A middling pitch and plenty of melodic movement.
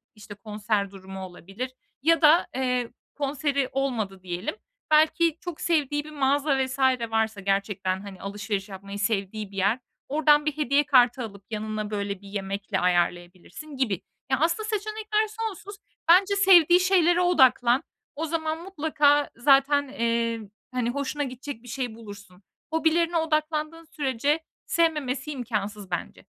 No: very high, 260 Hz; wide, 7.0 semitones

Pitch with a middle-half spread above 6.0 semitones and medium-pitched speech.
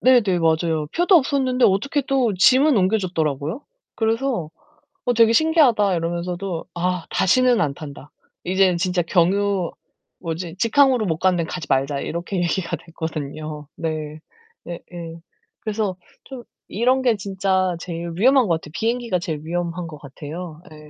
No: wide, 5.6 semitones; medium, 180 Hz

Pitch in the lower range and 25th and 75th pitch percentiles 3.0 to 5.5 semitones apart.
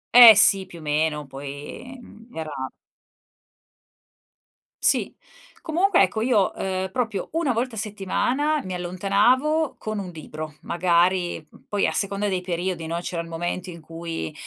No: high, 190 Hz; average, 5.1 semitones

